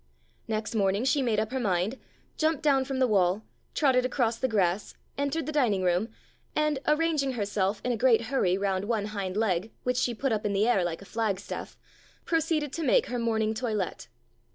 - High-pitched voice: Yes, high, 225 Hz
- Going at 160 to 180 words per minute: No, average, 200 wpm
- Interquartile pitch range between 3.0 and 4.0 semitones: No, average, 4.9 semitones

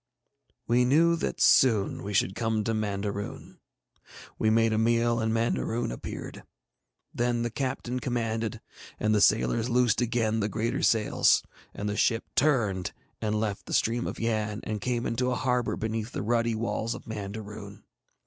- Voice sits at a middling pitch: No, low, 115 Hz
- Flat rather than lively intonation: Yes, narrow, 1.9 semitones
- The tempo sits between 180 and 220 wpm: No, average, 160 wpm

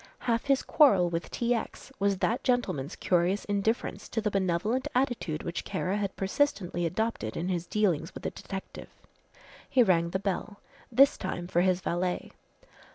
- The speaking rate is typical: Yes, average, 160 wpm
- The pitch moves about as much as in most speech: Yes, average, 4.6 semitones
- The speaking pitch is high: Yes, high, 195 Hz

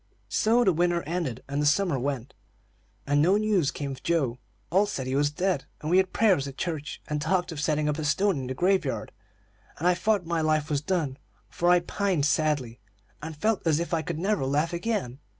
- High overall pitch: No, medium, 160 Hz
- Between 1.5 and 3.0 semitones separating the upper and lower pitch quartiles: No, average, 4.1 semitones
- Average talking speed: No, fast, 220 wpm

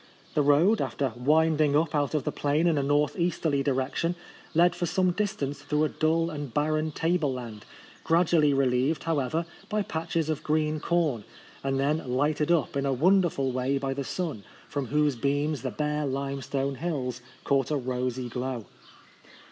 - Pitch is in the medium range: Yes, medium, 145 Hz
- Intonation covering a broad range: No, average, 3.0 semitones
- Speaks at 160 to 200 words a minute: Yes, average, 175 wpm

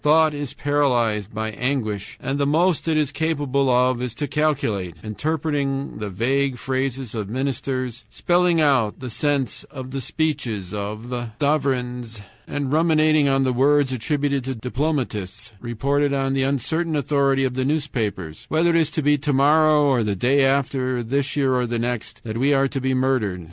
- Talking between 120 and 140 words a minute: No, average, 175 wpm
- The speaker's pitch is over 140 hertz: No, low, 135 Hz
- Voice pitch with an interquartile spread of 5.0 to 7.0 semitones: No, average, 3.2 semitones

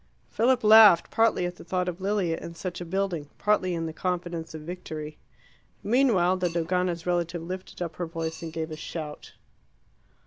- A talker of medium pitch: Yes, medium, 175 Hz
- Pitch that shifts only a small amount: Yes, narrow, 2.2 semitones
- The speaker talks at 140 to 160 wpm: No, average, 175 wpm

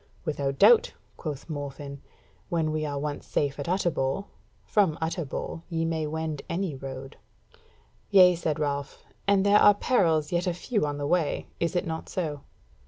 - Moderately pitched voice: Yes, medium, 160 Hz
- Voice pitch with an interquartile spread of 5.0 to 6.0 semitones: No, average, 3.7 semitones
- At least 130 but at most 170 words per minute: Yes, average, 165 wpm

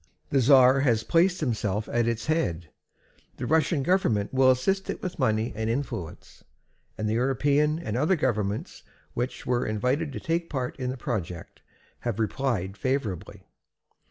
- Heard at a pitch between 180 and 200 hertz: No, low, 125 Hz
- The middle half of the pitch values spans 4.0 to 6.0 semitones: Yes, average, 4.9 semitones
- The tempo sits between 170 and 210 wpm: No, average, 155 wpm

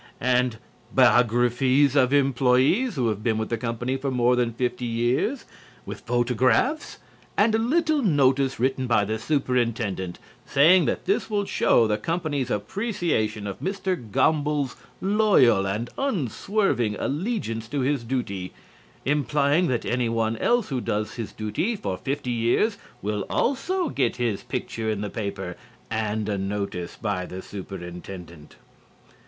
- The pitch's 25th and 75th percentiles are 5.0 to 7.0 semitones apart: Yes, wide, 5.6 semitones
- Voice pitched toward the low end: Yes, low, 125 Hz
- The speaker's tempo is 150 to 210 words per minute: No, average, 140 wpm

